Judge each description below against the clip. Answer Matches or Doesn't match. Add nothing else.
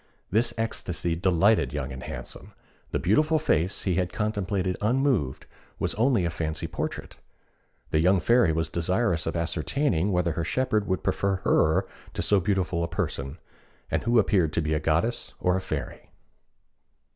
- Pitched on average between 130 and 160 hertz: Doesn't match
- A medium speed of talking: Matches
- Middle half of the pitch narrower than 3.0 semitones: Doesn't match